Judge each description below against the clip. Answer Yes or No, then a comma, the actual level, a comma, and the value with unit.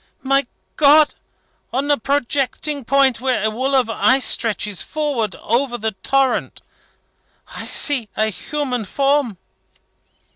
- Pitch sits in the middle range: No, very high, 265 Hz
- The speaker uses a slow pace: Yes, slow, 120 wpm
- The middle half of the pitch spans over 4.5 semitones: No, average, 3.6 semitones